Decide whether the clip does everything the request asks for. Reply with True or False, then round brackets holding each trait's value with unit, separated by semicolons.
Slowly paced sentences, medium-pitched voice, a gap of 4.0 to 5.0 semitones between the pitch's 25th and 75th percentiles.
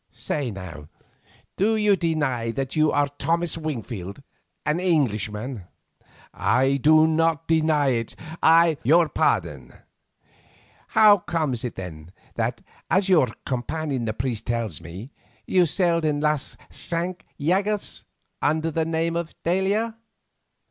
False (130 wpm; 155 Hz; 5.6 semitones)